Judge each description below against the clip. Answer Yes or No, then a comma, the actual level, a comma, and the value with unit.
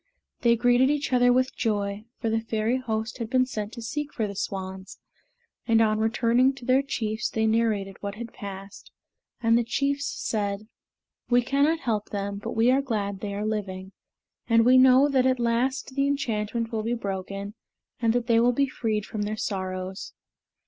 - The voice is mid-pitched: No, high, 225 Hz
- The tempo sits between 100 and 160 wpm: No, average, 185 wpm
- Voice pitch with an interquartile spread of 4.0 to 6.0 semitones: No, average, 3.5 semitones